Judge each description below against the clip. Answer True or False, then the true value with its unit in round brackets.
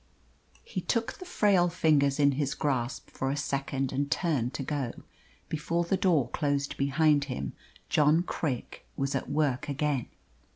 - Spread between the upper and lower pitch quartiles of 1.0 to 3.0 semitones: True (2.6 semitones)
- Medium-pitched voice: True (145 Hz)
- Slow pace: False (155 wpm)